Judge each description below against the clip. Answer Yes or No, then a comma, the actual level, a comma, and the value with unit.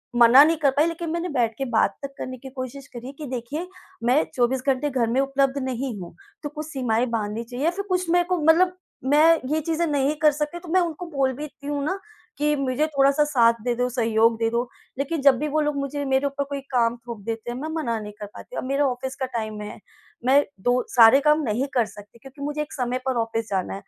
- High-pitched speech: Yes, very high, 270 Hz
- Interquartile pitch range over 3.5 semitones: Yes, average, 4.0 semitones